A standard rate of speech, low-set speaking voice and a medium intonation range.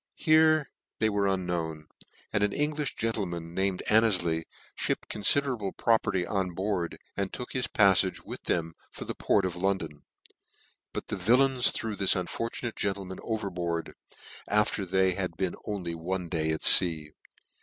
Yes: average, 155 wpm; very low, 95 Hz; average, 3.9 semitones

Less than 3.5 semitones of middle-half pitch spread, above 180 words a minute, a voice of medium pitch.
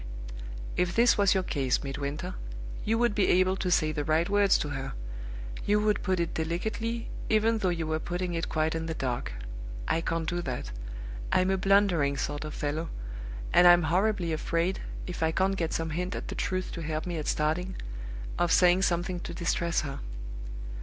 Yes: average, 3.1 semitones; average, 190 wpm; medium, 175 Hz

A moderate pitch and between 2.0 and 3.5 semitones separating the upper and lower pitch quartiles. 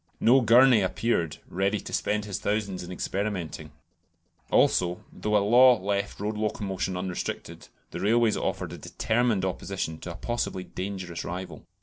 No: low, 100 Hz; average, 2.9 semitones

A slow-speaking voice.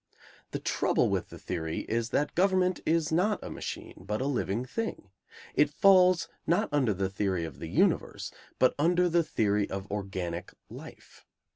No: average, 165 wpm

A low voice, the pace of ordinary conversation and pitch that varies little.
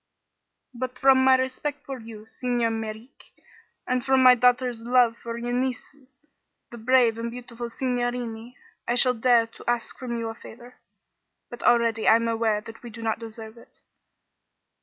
No: high, 240 Hz; average, 165 wpm; narrow, 1.8 semitones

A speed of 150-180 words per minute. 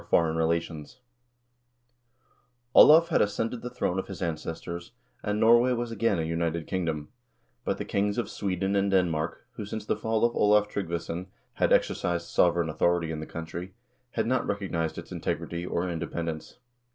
Yes: average, 165 wpm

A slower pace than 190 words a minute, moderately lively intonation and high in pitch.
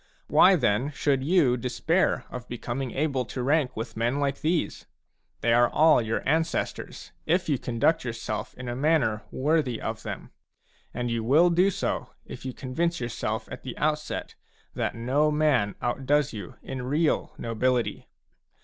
No: average, 160 wpm; average, 4.4 semitones; low, 130 Hz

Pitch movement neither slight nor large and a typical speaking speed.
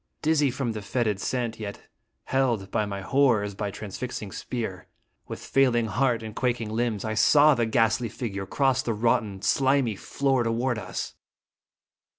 Yes: average, 3.4 semitones; average, 165 wpm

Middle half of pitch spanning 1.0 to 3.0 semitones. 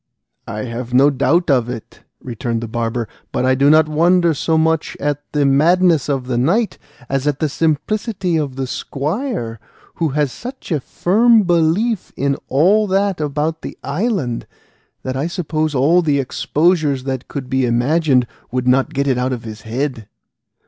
No: average, 4.7 semitones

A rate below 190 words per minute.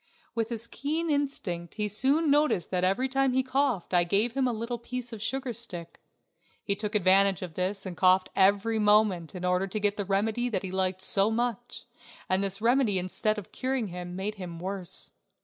No: average, 200 wpm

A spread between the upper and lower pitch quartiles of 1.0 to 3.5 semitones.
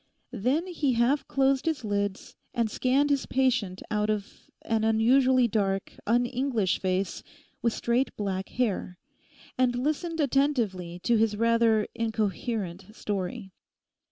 No: average, 4.1 semitones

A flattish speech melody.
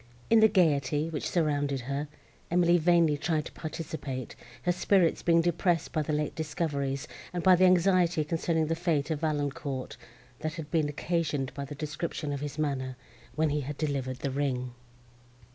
No: average, 3.0 semitones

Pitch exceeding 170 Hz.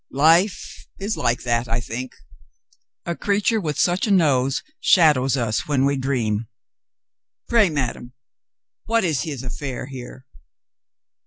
No: medium, 140 Hz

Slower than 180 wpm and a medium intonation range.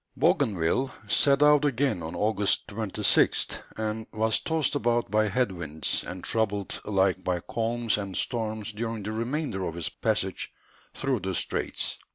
Yes: average, 150 wpm; average, 3.8 semitones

